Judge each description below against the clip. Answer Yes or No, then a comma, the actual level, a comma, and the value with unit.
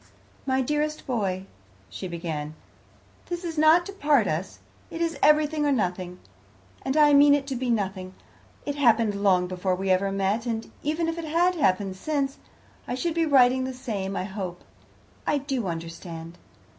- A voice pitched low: No, high, 245 Hz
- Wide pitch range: Yes, wide, 7.9 semitones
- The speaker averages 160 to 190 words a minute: Yes, average, 170 wpm